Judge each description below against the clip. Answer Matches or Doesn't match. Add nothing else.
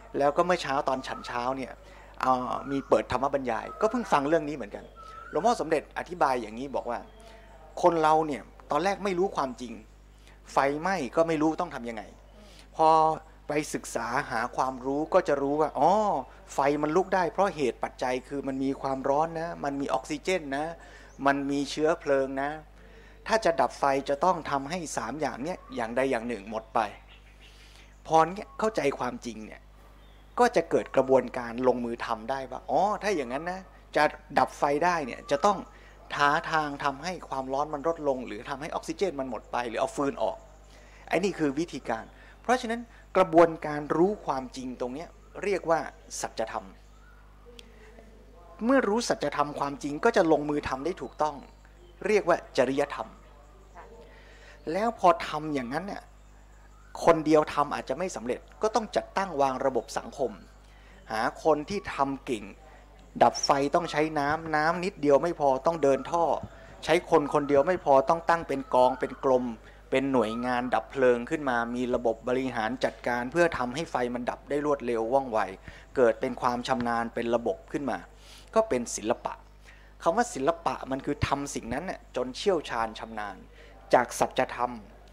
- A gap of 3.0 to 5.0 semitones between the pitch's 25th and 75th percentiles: Matches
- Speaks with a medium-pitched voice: Matches